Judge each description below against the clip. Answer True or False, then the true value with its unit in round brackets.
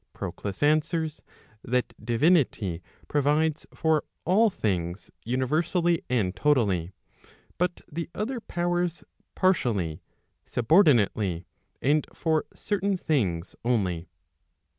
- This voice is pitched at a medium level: True (145 Hz)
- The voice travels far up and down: True (8.4 semitones)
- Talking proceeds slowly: True (95 wpm)